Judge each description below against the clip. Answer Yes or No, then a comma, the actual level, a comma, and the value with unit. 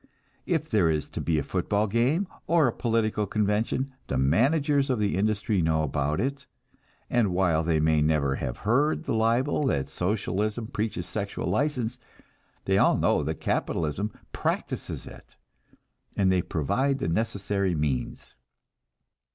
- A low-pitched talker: Yes, low, 105 Hz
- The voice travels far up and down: Yes, wide, 6.8 semitones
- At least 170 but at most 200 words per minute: No, average, 145 wpm